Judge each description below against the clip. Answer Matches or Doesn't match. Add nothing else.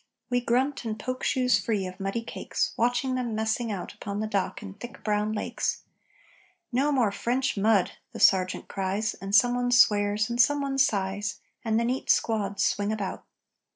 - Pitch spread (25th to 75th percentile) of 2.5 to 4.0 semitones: Matches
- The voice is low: Doesn't match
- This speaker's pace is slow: Doesn't match